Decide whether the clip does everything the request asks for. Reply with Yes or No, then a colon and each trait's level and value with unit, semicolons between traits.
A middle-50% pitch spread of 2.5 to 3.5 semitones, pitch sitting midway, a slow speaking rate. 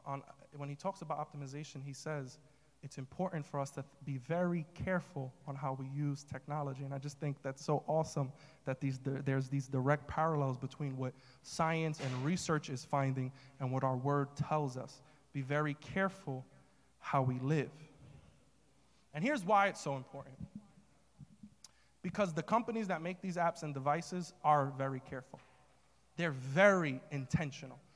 No: average, 2.9 semitones; medium, 145 Hz; average, 160 wpm